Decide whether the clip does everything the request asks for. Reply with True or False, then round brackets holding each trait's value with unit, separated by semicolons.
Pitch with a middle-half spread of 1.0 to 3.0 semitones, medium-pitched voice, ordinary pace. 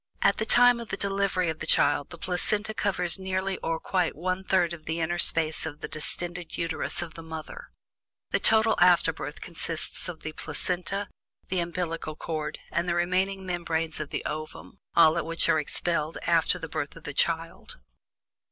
True (2.6 semitones; 170 Hz; 180 wpm)